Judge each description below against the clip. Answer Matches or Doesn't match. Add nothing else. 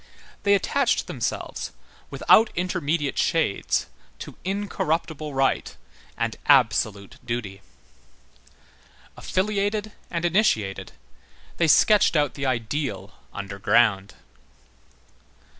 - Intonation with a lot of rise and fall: Matches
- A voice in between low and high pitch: Matches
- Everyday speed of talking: Doesn't match